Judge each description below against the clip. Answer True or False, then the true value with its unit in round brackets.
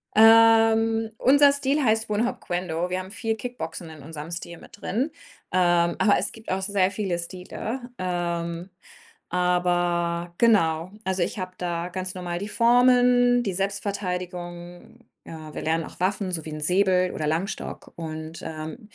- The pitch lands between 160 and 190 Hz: True (185 Hz)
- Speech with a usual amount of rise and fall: True (4.3 semitones)